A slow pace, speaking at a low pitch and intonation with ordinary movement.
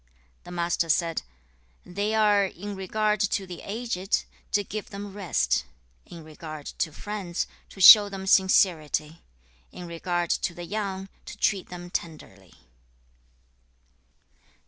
No: slow, 125 wpm; medium, 185 Hz; average, 3.2 semitones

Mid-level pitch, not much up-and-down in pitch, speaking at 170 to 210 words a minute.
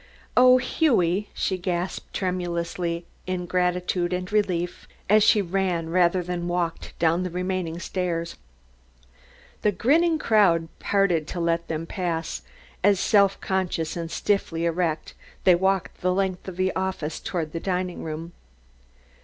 No: medium, 180 Hz; narrow, 2.1 semitones; slow, 135 wpm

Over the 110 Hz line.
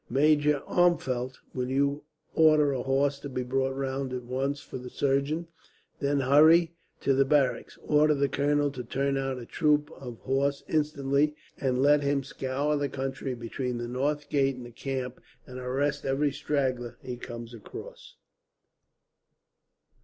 Yes: low, 135 Hz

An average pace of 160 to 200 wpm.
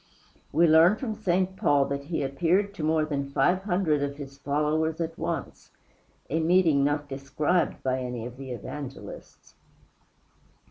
No: average, 150 wpm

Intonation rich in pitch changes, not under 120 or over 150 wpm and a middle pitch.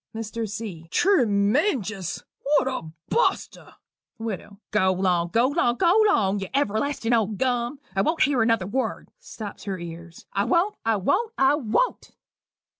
No: wide, 6.0 semitones; average, 145 wpm; high, 225 Hz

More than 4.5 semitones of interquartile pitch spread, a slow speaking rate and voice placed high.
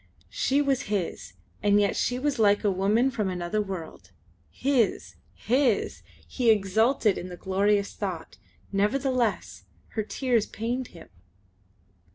No: average, 4.2 semitones; slow, 130 wpm; high, 210 Hz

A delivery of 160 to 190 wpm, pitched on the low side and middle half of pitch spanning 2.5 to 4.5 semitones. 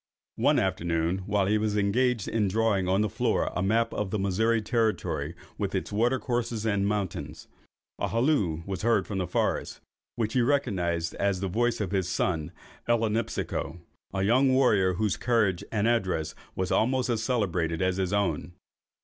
Yes: average, 170 wpm; low, 105 Hz; average, 3.8 semitones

